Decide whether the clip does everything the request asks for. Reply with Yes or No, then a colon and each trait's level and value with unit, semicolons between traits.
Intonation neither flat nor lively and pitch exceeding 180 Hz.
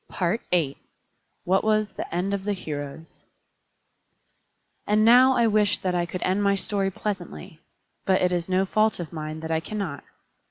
Yes: average, 3.5 semitones; high, 190 Hz